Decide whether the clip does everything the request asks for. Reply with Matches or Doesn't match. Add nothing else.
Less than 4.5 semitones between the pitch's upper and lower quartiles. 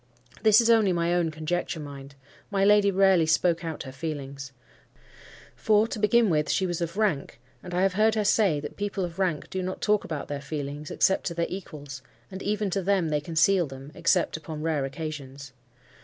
Doesn't match